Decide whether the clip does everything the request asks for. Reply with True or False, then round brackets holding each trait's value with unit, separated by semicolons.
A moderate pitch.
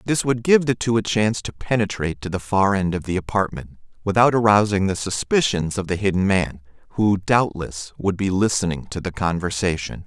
False (100 Hz)